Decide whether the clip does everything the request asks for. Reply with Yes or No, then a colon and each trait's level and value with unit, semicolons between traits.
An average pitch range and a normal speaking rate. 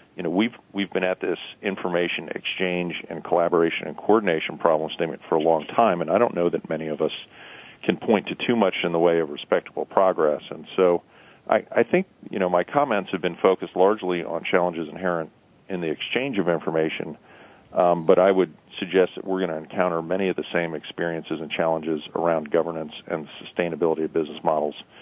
No: narrow, 1.9 semitones; average, 195 wpm